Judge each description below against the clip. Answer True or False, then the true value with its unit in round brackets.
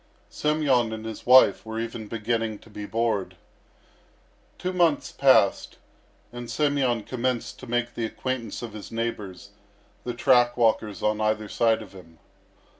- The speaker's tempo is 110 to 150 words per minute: True (145 wpm)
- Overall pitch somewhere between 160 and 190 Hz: False (115 Hz)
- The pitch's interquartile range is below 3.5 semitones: True (2.4 semitones)